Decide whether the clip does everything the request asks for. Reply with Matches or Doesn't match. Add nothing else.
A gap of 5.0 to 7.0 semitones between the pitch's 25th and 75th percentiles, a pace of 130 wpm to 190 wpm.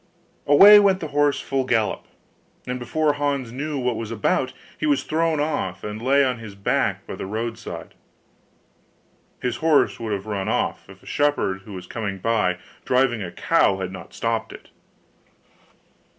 Matches